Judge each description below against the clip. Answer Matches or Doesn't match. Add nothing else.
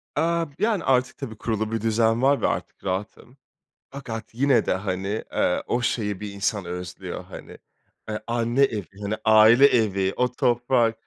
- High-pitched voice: Doesn't match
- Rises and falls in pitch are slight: Doesn't match